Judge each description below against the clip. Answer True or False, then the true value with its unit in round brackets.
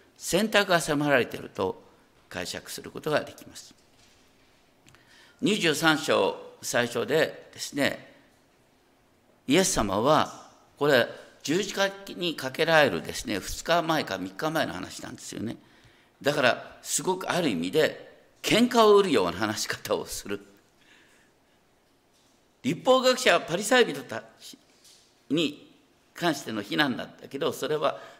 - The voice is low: False (180 Hz)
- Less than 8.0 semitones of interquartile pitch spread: False (8.9 semitones)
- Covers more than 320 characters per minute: False (250 characters per minute)